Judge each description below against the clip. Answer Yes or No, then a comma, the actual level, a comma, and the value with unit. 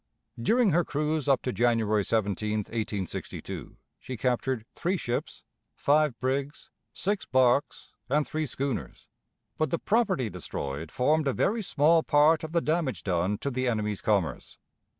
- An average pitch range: No, wide, 6.1 semitones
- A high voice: No, low, 130 Hz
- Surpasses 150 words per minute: No, average, 145 wpm